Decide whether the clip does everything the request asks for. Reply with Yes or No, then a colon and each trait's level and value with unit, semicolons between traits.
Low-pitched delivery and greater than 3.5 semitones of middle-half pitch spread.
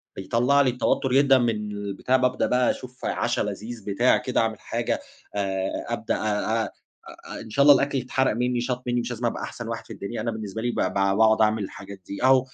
No: low, 115 Hz; average, 3.0 semitones